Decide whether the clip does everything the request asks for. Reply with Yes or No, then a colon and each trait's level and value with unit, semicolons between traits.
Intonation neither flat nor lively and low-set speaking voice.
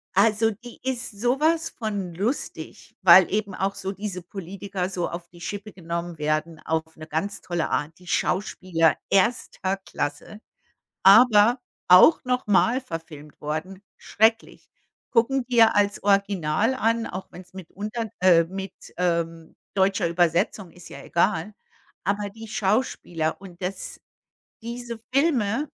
No: average, 4.5 semitones; high, 195 Hz